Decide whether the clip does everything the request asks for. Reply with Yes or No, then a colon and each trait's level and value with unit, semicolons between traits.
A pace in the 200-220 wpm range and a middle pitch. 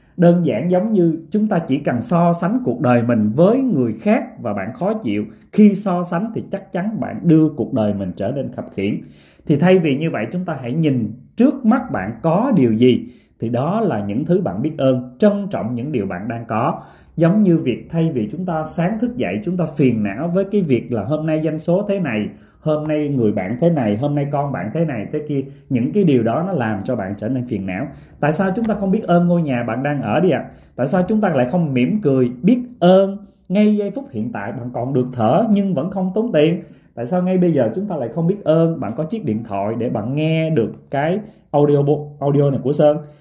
No: fast, 250 wpm; medium, 160 Hz